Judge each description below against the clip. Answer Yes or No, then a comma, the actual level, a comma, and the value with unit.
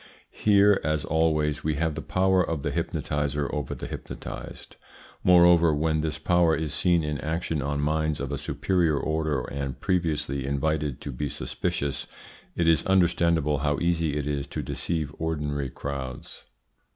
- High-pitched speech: No, very low, 75 Hz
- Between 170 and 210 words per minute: No, average, 155 wpm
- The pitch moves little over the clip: Yes, narrow, 2.3 semitones